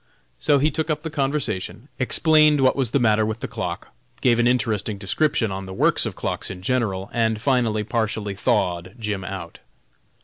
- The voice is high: No, low, 115 Hz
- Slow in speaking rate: No, average, 180 wpm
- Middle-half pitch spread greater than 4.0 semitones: Yes, average, 5.0 semitones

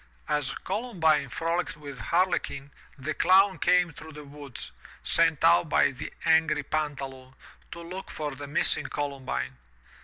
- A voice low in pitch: No, medium, 150 Hz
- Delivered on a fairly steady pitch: No, average, 3.3 semitones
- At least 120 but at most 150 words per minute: Yes, average, 140 wpm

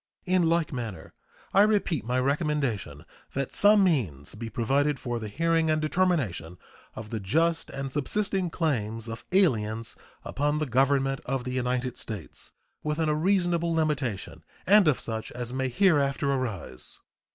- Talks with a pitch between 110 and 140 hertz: Yes, low, 135 Hz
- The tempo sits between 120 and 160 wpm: Yes, average, 150 wpm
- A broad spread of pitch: Yes, wide, 6.1 semitones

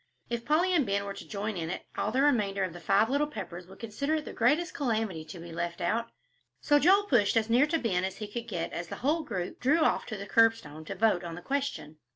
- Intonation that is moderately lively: No, wide, 7.5 semitones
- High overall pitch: Yes, high, 220 Hz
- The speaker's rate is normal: No, fast, 255 wpm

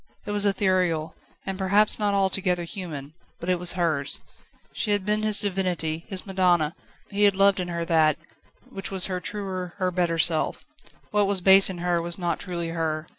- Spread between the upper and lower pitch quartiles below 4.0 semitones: Yes, narrow, 2.5 semitones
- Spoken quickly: No, average, 185 wpm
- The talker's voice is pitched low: No, medium, 180 Hz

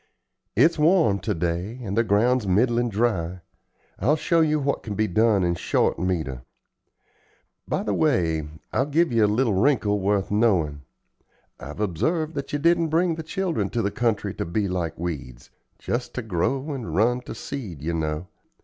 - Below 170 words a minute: No, average, 175 wpm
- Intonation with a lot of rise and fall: Yes, wide, 7.4 semitones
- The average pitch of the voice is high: No, low, 105 Hz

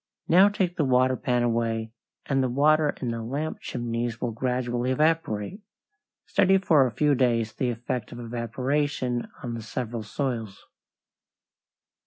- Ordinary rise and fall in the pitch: Yes, average, 3.7 semitones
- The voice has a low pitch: Yes, low, 125 Hz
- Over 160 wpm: No, average, 145 wpm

